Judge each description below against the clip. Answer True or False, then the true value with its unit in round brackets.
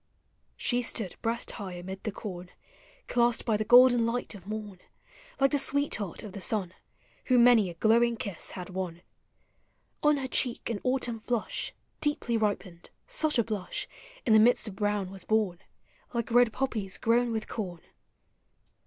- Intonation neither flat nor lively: True (3.9 semitones)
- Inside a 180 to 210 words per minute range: False (165 wpm)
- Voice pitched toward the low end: False (220 Hz)